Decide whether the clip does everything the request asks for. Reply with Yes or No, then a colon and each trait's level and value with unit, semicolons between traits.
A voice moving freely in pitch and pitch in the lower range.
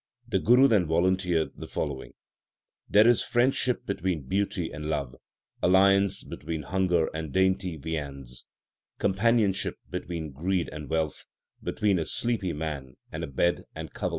No: average, 4.1 semitones; very low, 90 Hz